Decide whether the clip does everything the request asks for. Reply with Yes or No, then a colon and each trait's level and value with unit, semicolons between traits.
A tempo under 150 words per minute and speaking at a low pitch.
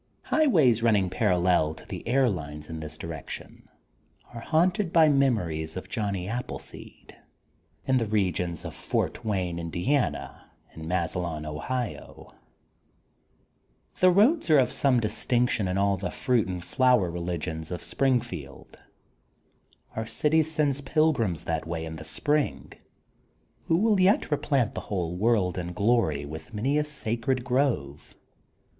Yes: average, 140 wpm; low, 105 Hz